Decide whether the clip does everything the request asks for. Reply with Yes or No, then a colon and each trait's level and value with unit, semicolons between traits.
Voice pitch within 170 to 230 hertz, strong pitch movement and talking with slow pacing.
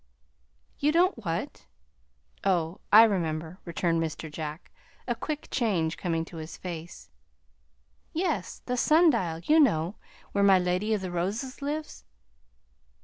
Yes: medium, 185 Hz; wide, 7.1 semitones; slow, 130 wpm